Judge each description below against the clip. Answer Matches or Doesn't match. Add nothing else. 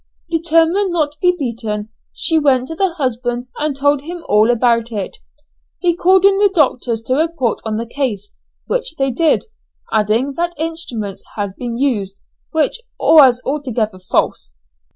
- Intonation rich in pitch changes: Matches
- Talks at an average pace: Matches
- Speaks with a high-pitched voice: Matches